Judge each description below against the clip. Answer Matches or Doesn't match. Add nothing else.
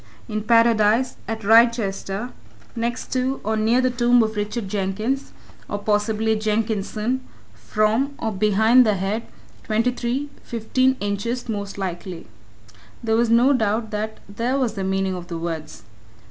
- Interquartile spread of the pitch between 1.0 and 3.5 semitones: Matches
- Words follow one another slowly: Doesn't match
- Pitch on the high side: Matches